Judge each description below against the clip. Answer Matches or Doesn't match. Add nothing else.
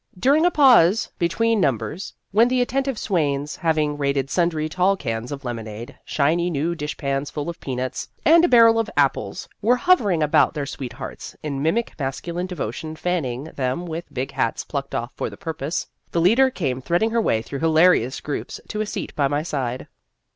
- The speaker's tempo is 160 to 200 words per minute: Matches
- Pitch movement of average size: Doesn't match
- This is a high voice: Doesn't match